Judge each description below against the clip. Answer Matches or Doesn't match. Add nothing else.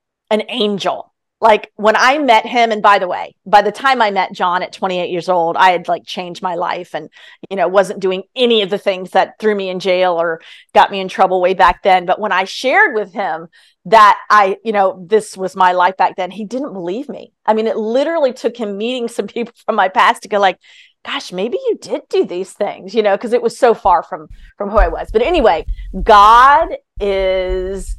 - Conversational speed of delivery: Doesn't match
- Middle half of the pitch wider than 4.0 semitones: Doesn't match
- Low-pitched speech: Doesn't match